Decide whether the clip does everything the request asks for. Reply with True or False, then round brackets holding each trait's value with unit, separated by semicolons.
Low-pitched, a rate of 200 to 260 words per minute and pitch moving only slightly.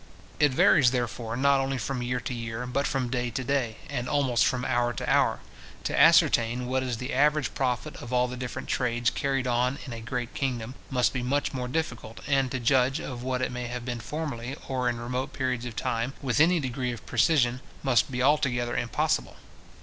True (125 Hz; 205 wpm; 1.9 semitones)